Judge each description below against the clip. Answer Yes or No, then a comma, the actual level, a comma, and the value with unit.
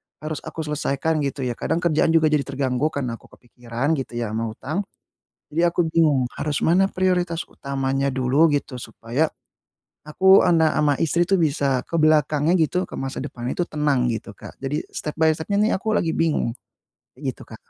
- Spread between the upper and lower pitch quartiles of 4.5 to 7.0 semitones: No, average, 3.6 semitones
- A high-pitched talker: No, medium, 150 Hz